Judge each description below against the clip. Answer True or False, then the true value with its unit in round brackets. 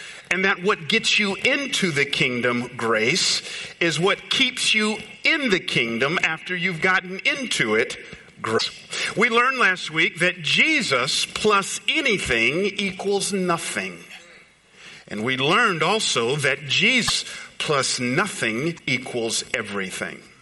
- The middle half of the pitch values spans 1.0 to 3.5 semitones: False (5.0 semitones)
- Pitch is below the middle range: False (185 Hz)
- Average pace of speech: False (125 wpm)